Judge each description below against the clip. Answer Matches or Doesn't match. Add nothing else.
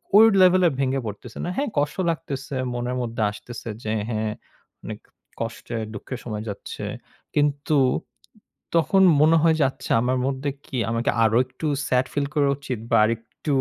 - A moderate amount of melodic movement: Matches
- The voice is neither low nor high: Doesn't match